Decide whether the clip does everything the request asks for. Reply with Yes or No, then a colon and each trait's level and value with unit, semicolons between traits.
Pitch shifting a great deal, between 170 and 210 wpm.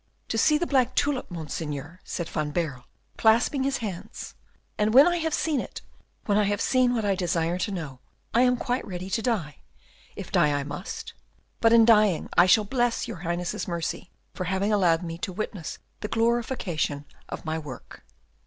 Yes: wide, 6.1 semitones; average, 185 wpm